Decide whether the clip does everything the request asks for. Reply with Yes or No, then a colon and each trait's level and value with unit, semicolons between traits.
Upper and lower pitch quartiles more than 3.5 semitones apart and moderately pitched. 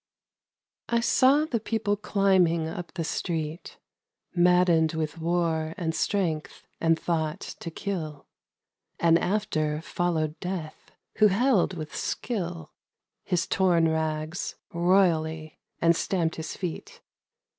No: average, 3.0 semitones; medium, 170 Hz